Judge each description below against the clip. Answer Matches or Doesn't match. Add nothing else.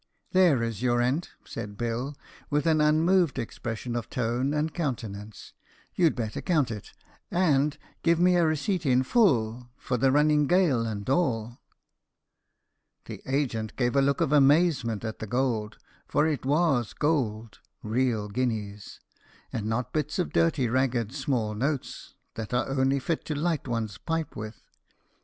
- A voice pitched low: Matches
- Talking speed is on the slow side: Doesn't match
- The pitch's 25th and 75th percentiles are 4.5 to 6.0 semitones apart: Matches